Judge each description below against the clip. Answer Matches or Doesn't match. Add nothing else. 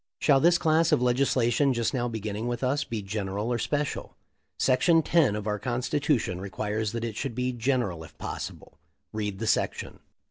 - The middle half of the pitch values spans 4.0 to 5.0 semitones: Matches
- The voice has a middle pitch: Doesn't match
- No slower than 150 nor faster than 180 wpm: Matches